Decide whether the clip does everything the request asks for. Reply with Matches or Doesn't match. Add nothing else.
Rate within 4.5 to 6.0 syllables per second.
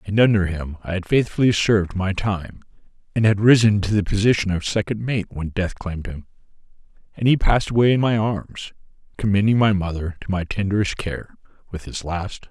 Matches